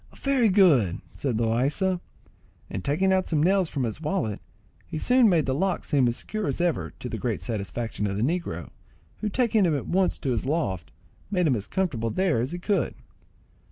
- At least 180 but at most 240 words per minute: Yes, average, 195 wpm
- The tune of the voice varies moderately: No, wide, 8.2 semitones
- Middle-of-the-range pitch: Yes, medium, 155 Hz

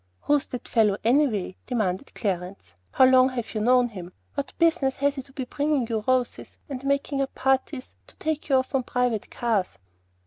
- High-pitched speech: Yes, very high, 255 Hz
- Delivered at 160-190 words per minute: Yes, average, 185 wpm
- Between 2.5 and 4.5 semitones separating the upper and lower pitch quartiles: Yes, average, 3.8 semitones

